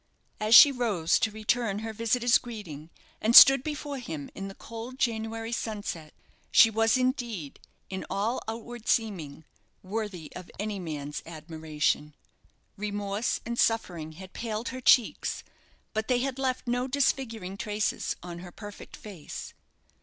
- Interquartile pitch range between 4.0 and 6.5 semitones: Yes, average, 4.7 semitones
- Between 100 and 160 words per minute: Yes, average, 140 wpm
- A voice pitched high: Yes, high, 215 Hz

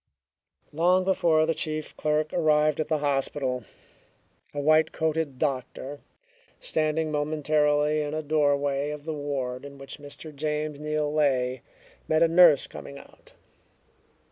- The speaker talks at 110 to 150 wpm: Yes, slow, 135 wpm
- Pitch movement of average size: No, narrow, 1.6 semitones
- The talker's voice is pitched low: No, medium, 150 Hz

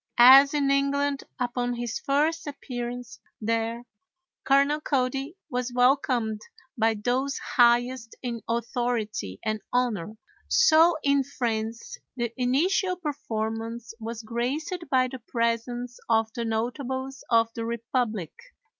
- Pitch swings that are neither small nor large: Yes, average, 3.1 semitones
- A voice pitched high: Yes, high, 245 Hz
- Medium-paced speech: No, slow, 115 wpm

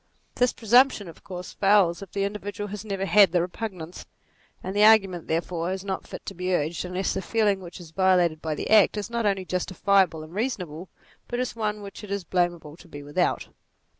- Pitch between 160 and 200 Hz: Yes, high, 190 Hz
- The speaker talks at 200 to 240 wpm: Yes, fast, 205 wpm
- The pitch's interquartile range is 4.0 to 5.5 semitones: No, average, 2.9 semitones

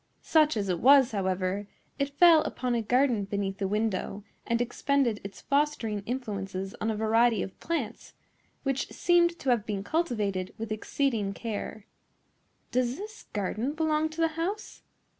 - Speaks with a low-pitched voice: No, high, 235 Hz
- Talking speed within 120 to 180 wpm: Yes, average, 155 wpm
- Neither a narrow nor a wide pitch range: No, wide, 5.9 semitones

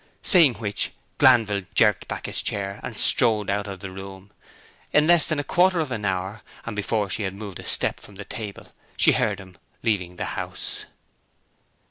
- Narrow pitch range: No, average, 3.0 semitones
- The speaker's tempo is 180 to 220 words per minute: Yes, average, 185 wpm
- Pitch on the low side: Yes, low, 105 Hz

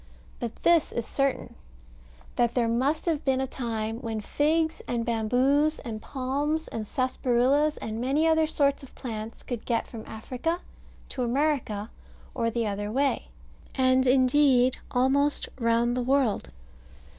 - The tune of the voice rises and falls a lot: No, average, 3.5 semitones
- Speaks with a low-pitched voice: No, very high, 255 Hz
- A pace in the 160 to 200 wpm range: No, average, 145 wpm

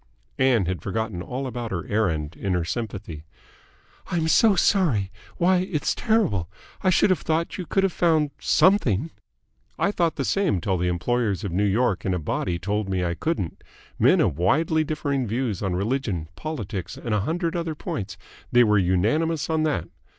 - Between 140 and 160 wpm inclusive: No, average, 180 wpm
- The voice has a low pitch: Yes, low, 115 Hz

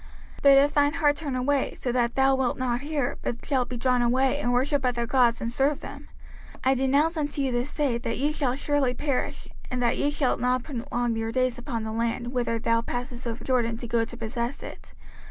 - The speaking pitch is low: No, very high, 255 Hz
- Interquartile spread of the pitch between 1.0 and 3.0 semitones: Yes, average, 2.7 semitones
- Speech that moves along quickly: Yes, fast, 225 wpm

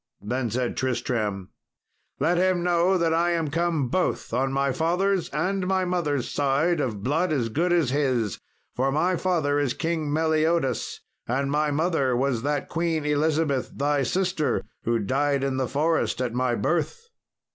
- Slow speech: No, average, 160 wpm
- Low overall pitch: No, medium, 145 Hz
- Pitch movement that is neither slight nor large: Yes, average, 4.5 semitones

